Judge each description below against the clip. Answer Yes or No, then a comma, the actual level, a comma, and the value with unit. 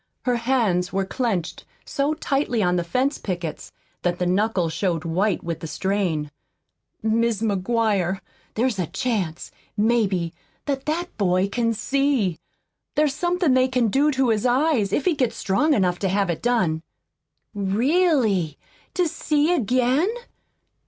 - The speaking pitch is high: Yes, high, 220 Hz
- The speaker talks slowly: No, average, 145 wpm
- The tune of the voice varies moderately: No, wide, 6.3 semitones